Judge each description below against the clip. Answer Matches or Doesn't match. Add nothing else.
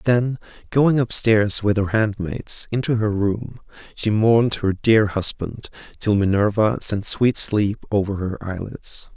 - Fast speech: Doesn't match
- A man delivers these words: Matches